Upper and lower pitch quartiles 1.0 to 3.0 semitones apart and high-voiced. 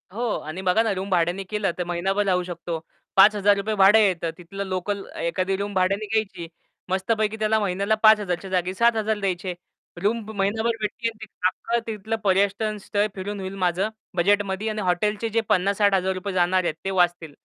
Yes: narrow, 2.5 semitones; high, 195 Hz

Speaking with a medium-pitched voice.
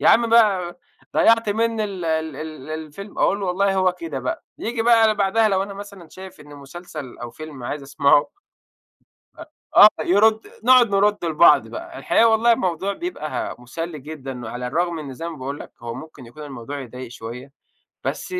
Yes: medium, 170 Hz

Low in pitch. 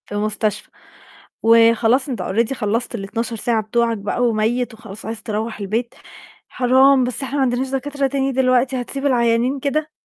No: high, 240 Hz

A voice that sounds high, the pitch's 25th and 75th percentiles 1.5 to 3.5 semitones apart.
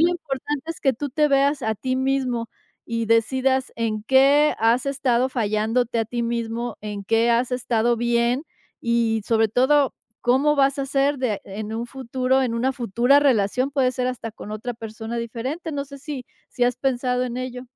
Yes: very high, 250 Hz; average, 2.7 semitones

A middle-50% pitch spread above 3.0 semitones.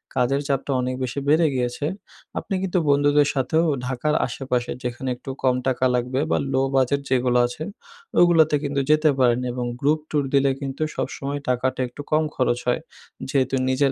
No: narrow, 2.5 semitones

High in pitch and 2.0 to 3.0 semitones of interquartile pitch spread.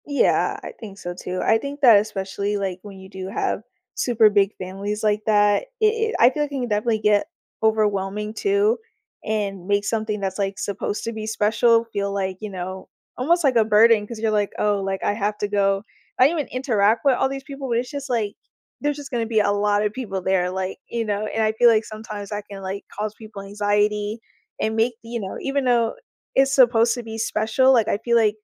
Yes: high, 215 Hz; average, 2.7 semitones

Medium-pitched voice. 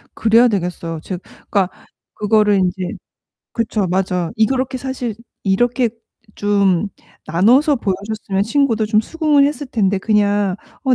No: high, 210 Hz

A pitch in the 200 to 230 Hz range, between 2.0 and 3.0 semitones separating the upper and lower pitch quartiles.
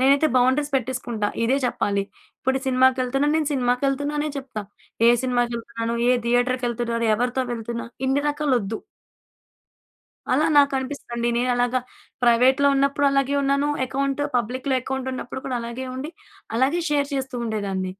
No: very high, 255 Hz; narrow, 2.5 semitones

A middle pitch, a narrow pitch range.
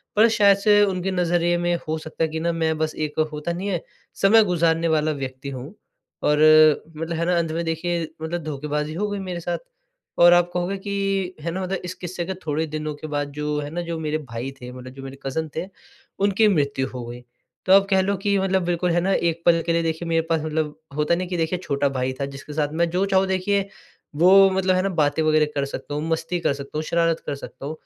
No: medium, 165 Hz; average, 3.5 semitones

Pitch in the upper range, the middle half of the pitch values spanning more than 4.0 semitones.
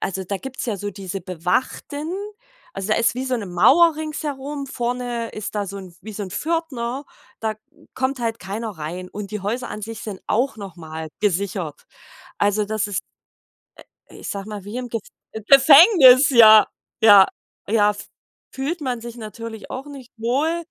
Yes: high, 225 Hz; average, 4.7 semitones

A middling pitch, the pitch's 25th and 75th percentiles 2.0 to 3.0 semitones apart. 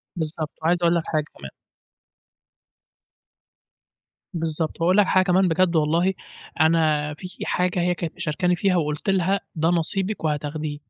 Yes: medium, 165 Hz; average, 2.7 semitones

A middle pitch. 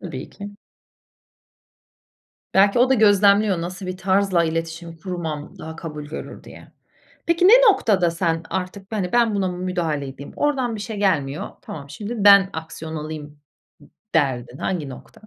Yes: medium, 180 Hz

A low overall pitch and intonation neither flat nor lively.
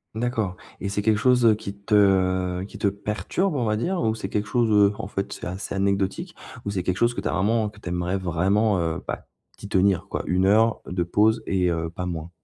Yes: low, 100 Hz; average, 3.0 semitones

